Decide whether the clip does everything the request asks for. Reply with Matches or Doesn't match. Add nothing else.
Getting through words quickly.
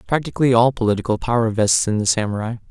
Doesn't match